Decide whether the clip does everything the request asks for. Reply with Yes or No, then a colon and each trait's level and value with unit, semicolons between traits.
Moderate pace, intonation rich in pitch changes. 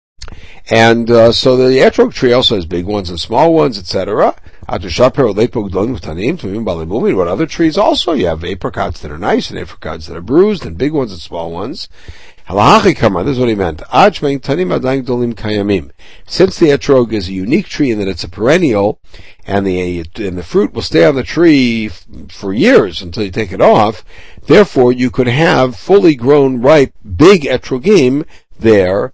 Yes: average, 165 wpm; wide, 6.2 semitones